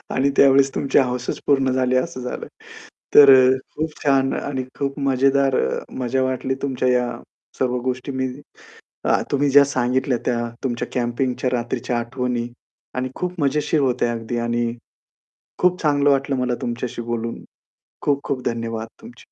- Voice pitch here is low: Yes, low, 130 Hz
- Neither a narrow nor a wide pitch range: No, narrow, 2.1 semitones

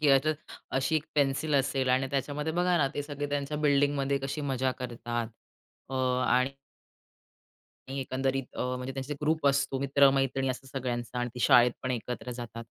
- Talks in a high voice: No, low, 135 Hz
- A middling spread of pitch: No, narrow, 1.9 semitones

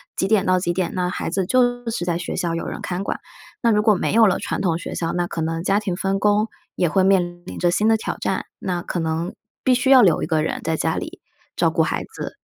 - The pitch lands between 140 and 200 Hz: Yes, medium, 185 Hz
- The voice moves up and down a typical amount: Yes, average, 3.3 semitones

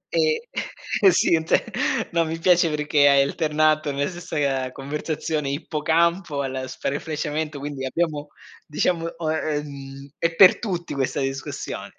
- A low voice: No, medium, 150 Hz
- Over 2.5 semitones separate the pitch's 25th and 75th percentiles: Yes, average, 2.9 semitones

